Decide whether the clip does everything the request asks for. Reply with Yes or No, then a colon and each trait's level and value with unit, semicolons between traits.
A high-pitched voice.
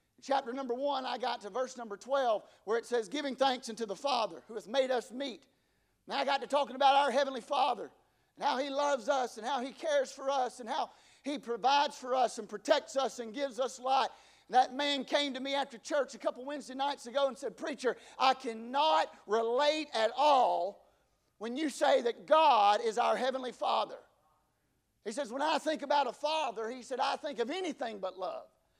Yes: very high, 270 Hz